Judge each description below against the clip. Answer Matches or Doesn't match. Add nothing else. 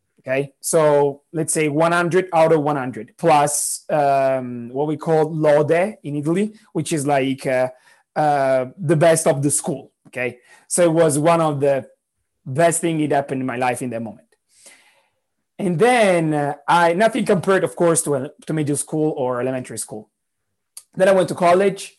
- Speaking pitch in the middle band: Matches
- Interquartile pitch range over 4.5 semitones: Doesn't match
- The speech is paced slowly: Doesn't match